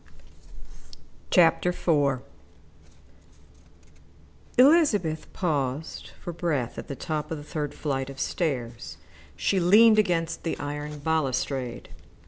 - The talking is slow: Yes, slow, 105 wpm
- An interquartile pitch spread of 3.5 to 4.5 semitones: Yes, average, 4.2 semitones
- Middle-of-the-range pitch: Yes, medium, 155 Hz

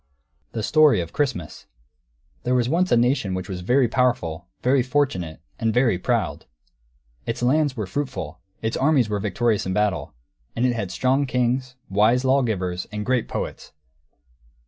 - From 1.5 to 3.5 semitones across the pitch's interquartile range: No, average, 5.1 semitones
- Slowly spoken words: No, average, 155 wpm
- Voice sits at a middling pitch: No, low, 120 Hz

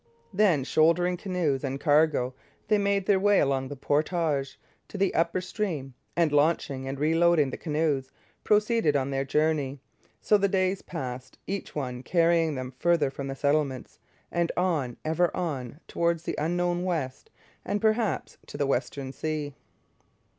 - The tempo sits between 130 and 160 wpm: Yes, average, 155 wpm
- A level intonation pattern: No, average, 4.5 semitones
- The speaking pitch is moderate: Yes, medium, 155 Hz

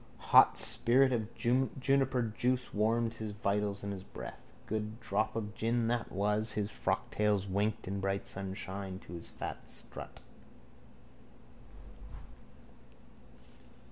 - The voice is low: Yes, low, 105 Hz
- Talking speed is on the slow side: Yes, slow, 115 wpm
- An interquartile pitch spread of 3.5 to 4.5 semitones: No, average, 2.8 semitones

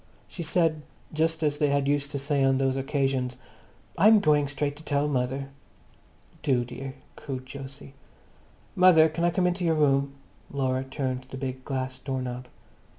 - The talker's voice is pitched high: No, medium, 140 Hz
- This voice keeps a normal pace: Yes, average, 170 wpm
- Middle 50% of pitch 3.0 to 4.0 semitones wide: No, narrow, 2.5 semitones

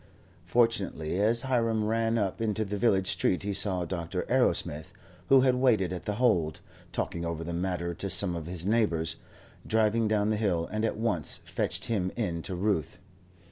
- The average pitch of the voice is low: Yes, low, 100 Hz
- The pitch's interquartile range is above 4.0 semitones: Yes, average, 4.5 semitones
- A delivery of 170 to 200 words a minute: Yes, average, 180 wpm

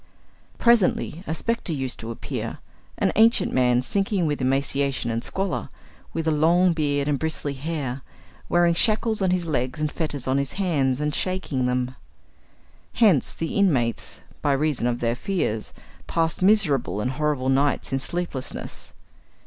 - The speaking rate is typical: Yes, average, 150 wpm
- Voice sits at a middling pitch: Yes, medium, 150 Hz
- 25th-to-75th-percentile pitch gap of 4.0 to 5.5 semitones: Yes, average, 5.1 semitones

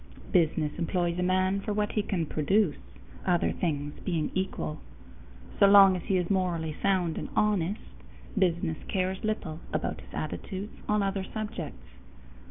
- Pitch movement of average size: Yes, average, 3.1 semitones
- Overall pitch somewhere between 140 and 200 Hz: Yes, medium, 185 Hz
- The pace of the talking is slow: No, average, 150 wpm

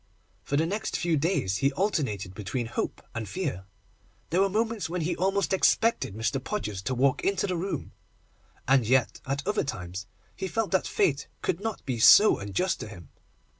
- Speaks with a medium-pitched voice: Yes, medium, 145 Hz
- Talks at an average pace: Yes, average, 180 wpm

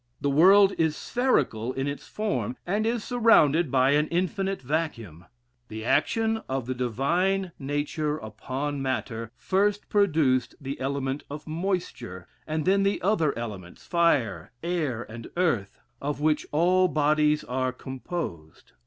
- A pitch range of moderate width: No, wide, 6.0 semitones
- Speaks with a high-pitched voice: No, medium, 150 Hz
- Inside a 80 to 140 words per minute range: Yes, slow, 135 wpm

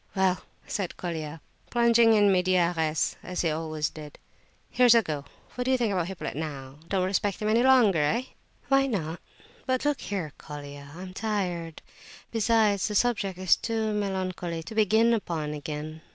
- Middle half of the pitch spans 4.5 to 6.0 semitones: Yes, wide, 5.6 semitones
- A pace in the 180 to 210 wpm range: No, average, 165 wpm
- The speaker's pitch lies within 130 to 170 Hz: No, medium, 185 Hz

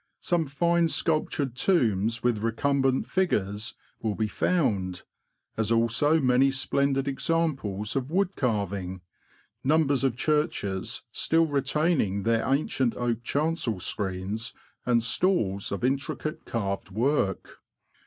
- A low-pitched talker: Yes, low, 125 Hz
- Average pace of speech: No, slow, 115 wpm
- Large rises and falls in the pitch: Yes, wide, 6.0 semitones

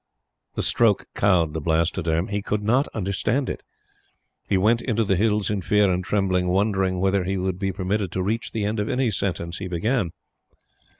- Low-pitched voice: Yes, very low, 95 Hz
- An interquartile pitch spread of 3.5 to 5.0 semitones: No, narrow, 2.6 semitones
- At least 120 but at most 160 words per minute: No, average, 185 wpm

